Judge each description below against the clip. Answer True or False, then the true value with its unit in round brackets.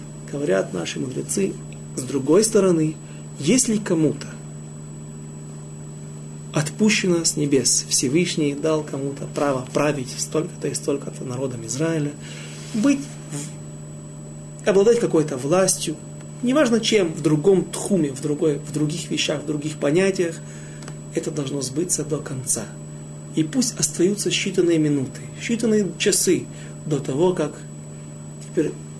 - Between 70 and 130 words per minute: True (110 wpm)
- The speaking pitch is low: False (145 Hz)